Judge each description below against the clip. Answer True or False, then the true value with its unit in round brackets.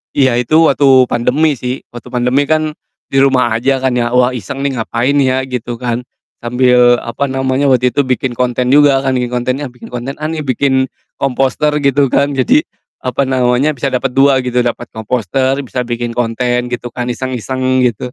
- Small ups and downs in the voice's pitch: True (1.9 semitones)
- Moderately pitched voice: False (130 Hz)